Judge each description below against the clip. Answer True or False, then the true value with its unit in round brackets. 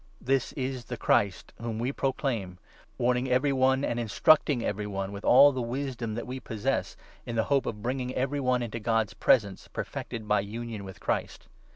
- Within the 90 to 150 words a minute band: False (190 wpm)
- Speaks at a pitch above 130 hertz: False (120 Hz)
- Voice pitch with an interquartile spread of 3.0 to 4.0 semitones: True (3.5 semitones)